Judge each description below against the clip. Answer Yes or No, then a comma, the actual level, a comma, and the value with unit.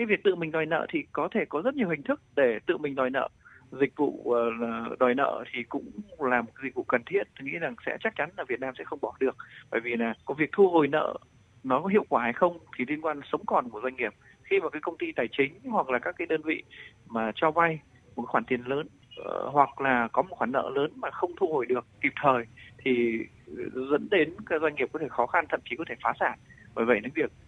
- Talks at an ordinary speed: No, fast, 260 wpm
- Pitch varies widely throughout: Yes, wide, 8.5 semitones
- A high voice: No, medium, 155 Hz